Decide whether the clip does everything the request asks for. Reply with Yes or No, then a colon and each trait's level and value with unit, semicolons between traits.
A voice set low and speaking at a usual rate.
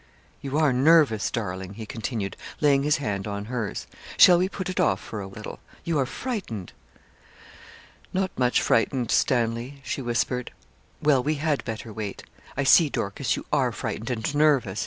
Yes: low, 125 Hz; average, 165 wpm